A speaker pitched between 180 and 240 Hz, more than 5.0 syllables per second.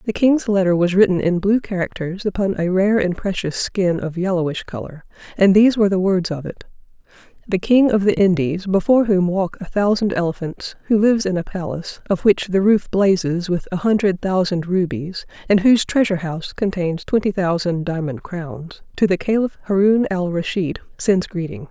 Yes: medium, 185 Hz; 5.3 syllables/s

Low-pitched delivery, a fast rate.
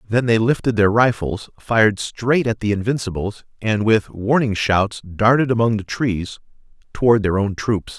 No: low, 110 Hz; average, 165 wpm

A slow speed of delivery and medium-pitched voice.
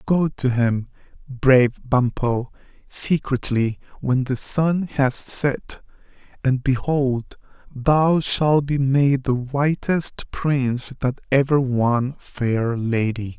No: slow, 110 wpm; low, 130 Hz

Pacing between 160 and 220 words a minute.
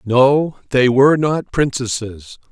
No: slow, 120 wpm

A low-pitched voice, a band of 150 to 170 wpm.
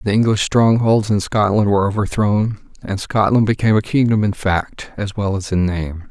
No: low, 105 Hz; average, 185 wpm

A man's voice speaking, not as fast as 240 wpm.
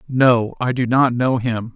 Yes: male; fast, 205 wpm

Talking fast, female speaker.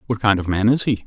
No: fast, 340 wpm; male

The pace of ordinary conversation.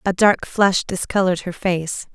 Yes: average, 170 wpm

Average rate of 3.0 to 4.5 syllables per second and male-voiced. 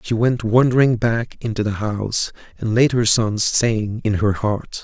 Yes: 4.3 syllables/s; male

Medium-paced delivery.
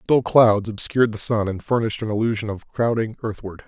Yes: average, 195 wpm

